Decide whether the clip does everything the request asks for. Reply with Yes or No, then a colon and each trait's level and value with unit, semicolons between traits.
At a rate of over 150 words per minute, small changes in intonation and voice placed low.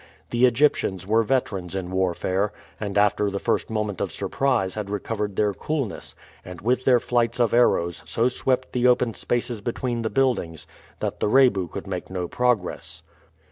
No: average, 170 wpm; average, 4.4 semitones; low, 110 Hz